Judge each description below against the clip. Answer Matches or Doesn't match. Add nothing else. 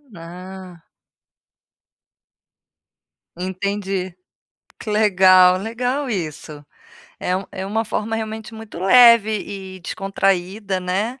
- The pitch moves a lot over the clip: Doesn't match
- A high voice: Matches